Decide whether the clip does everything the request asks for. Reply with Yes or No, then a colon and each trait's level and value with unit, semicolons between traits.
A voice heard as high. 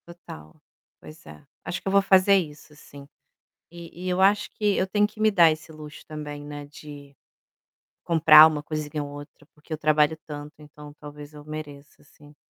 No: medium, 150 Hz